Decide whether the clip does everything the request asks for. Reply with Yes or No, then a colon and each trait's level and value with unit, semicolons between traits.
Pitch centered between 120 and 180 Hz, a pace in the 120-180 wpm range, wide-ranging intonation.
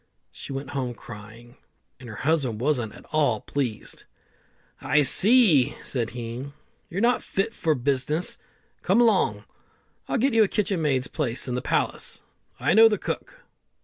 Yes: medium, 140 Hz; average, 155 wpm; wide, 7.8 semitones